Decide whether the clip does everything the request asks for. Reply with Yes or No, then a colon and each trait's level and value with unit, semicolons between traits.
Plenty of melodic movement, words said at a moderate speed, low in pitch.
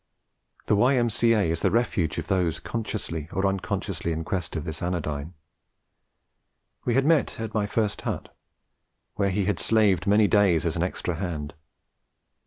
No: average, 4.5 semitones; average, 155 wpm; very low, 95 Hz